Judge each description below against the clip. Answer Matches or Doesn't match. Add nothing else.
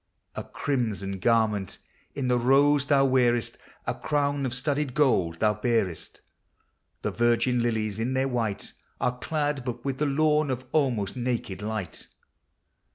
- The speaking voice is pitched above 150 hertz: Doesn't match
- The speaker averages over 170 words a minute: Doesn't match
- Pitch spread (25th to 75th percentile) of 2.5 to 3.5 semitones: Doesn't match